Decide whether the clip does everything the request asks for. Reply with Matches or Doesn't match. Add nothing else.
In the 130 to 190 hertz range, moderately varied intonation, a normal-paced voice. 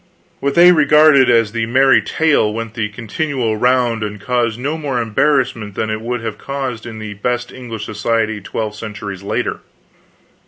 Doesn't match